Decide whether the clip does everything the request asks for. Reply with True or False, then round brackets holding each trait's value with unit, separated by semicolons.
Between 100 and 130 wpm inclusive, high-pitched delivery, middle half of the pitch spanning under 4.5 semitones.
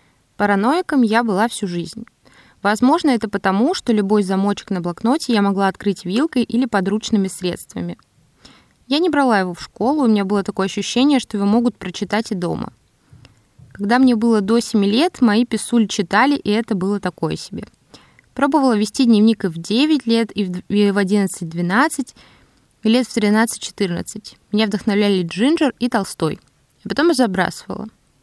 False (155 wpm; 210 Hz; 3.8 semitones)